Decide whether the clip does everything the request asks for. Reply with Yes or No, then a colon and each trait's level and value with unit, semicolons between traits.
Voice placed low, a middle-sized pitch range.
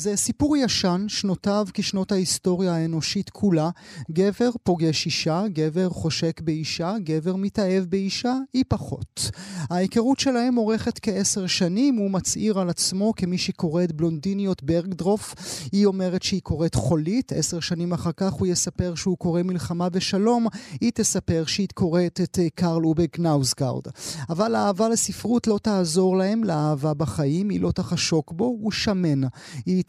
No: medium, 185 Hz; average, 3.4 semitones